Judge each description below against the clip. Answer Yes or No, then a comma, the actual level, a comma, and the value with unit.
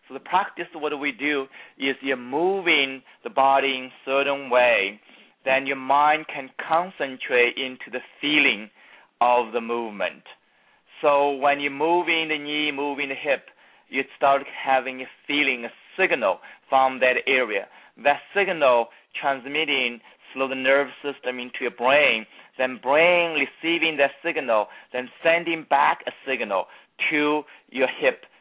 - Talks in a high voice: No, medium, 140 Hz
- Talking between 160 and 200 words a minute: No, average, 145 wpm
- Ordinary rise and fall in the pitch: No, narrow, 2.3 semitones